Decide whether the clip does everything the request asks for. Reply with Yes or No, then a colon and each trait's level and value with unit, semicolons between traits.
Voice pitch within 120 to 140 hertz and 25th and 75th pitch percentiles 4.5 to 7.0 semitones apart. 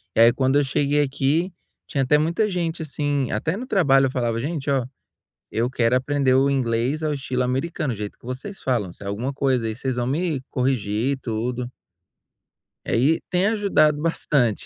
No: low, 135 Hz; average, 3.6 semitones